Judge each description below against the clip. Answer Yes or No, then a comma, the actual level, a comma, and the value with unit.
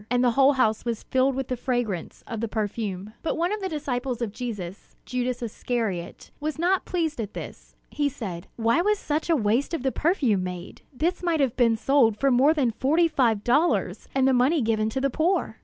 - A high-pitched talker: Yes, very high, 250 Hz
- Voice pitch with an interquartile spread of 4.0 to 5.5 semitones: Yes, average, 5.1 semitones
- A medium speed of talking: No, fast, 210 wpm